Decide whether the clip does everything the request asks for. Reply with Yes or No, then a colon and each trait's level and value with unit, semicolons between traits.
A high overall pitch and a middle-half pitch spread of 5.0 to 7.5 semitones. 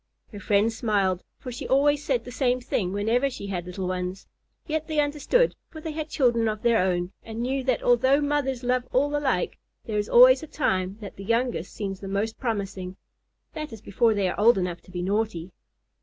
Yes: high, 225 Hz; wide, 5.5 semitones